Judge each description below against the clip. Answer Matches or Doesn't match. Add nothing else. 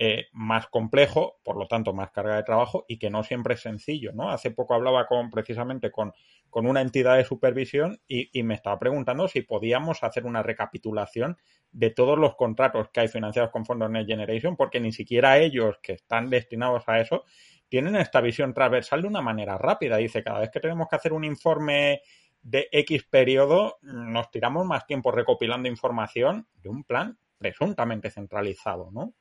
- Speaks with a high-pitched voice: Doesn't match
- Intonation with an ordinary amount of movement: Matches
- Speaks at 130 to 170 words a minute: Doesn't match